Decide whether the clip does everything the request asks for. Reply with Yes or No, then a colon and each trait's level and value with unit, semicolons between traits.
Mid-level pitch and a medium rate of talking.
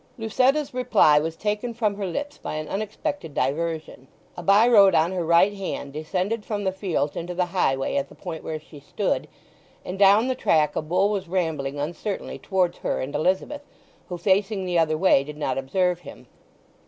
Yes: medium, 180 Hz; average, 190 wpm